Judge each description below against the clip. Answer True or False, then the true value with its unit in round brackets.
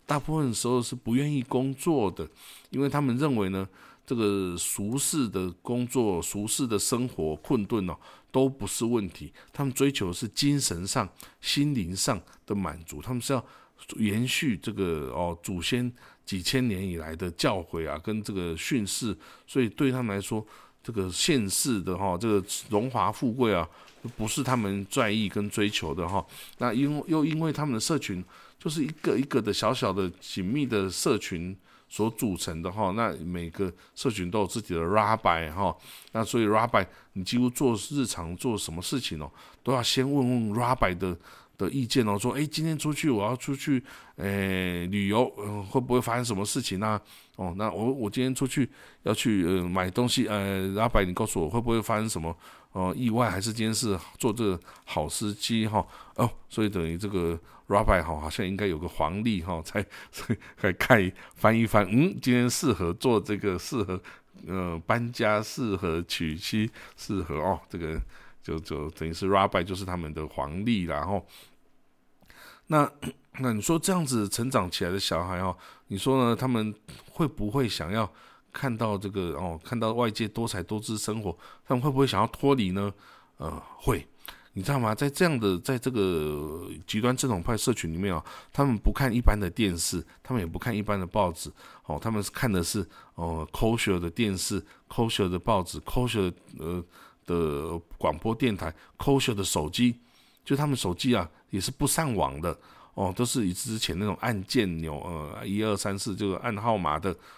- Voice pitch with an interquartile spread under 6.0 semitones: True (5.1 semitones)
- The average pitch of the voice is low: True (105 Hz)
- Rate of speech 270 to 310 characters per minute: True (275 characters per minute)